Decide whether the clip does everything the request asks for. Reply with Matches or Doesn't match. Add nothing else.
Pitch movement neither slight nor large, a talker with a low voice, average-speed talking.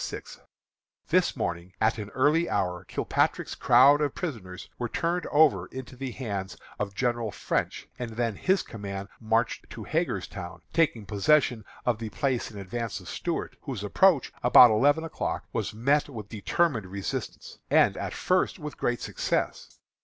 Doesn't match